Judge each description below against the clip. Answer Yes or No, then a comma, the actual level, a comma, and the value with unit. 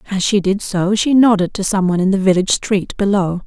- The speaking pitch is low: No, high, 195 Hz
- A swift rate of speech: Yes, fast, 225 wpm